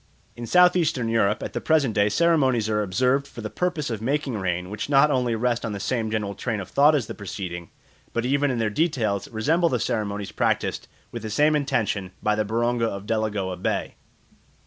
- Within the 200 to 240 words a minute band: Yes, fast, 205 wpm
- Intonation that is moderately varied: Yes, average, 4.9 semitones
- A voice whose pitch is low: Yes, low, 115 Hz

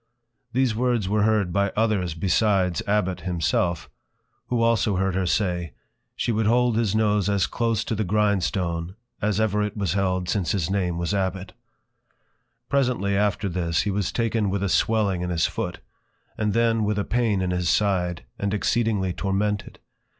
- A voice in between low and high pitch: No, low, 100 Hz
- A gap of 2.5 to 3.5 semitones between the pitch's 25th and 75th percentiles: Yes, average, 3.0 semitones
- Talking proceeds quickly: No, average, 170 wpm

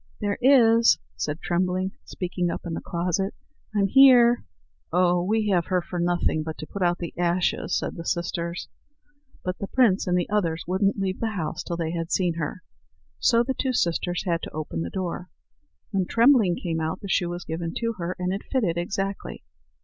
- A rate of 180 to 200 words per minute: Yes, average, 195 wpm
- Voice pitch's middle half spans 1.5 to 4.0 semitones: Yes, average, 2.9 semitones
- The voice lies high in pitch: No, medium, 180 Hz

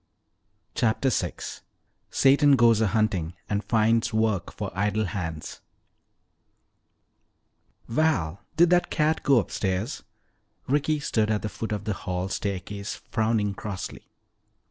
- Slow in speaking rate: Yes, slow, 120 wpm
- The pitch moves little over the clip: No, average, 3.4 semitones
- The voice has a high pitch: No, low, 110 Hz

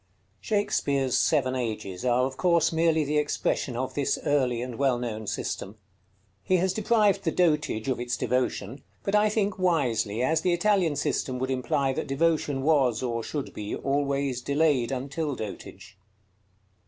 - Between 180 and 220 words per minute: No, average, 155 wpm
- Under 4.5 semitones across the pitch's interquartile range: No, average, 4.8 semitones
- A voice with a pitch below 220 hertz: Yes, medium, 140 Hz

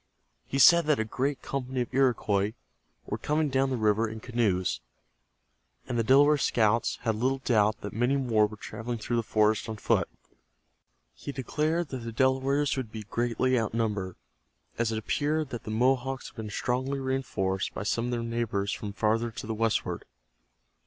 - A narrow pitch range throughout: No, average, 3.5 semitones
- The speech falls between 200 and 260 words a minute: No, average, 175 wpm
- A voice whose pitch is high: No, low, 120 Hz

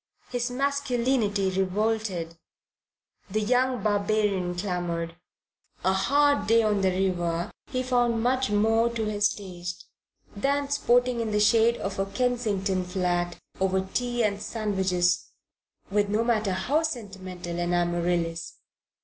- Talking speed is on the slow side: Yes, slow, 125 wpm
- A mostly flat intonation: No, average, 4.4 semitones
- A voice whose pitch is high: Yes, high, 205 Hz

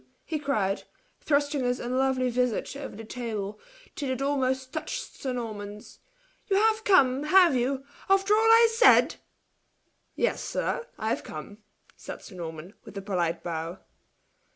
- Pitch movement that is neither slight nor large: No, wide, 6.0 semitones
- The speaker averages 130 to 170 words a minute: Yes, average, 150 wpm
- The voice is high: Yes, very high, 255 Hz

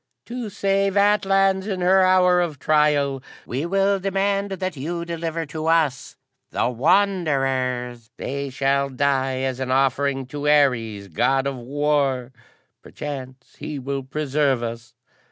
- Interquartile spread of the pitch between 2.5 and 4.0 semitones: No, wide, 5.6 semitones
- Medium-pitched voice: Yes, medium, 145 Hz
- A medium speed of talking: No, slow, 130 wpm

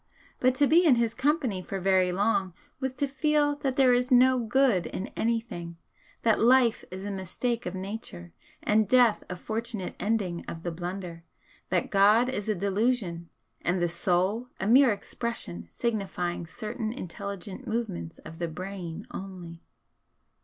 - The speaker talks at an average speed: Yes, average, 155 wpm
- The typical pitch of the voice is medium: No, high, 205 Hz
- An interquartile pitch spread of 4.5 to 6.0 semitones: Yes, average, 5.3 semitones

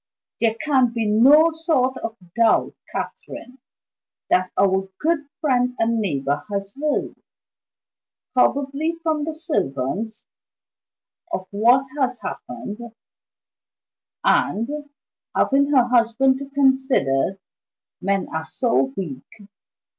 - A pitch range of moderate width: No, wide, 5.9 semitones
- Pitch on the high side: Yes, high, 245 Hz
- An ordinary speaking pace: No, slow, 100 wpm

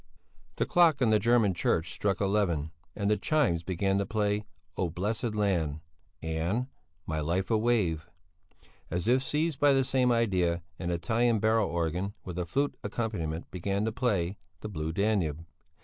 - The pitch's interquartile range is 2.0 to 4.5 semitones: No, average, 5.1 semitones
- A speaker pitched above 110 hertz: No, low, 100 Hz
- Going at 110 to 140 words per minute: No, average, 165 wpm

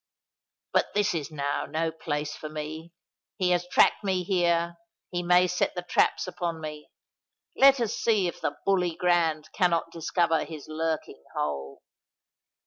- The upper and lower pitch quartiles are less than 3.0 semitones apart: Yes, narrow, 2.4 semitones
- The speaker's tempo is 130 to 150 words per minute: Yes, average, 145 wpm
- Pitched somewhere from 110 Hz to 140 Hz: No, medium, 170 Hz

